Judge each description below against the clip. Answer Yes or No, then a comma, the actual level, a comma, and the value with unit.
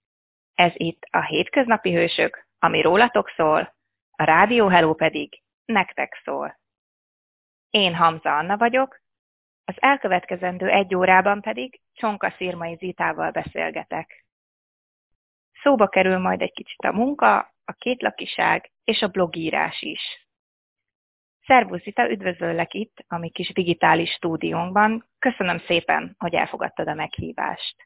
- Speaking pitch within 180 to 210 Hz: Yes, medium, 185 Hz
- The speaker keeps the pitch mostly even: No, average, 4.3 semitones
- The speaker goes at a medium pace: Yes, average, 120 wpm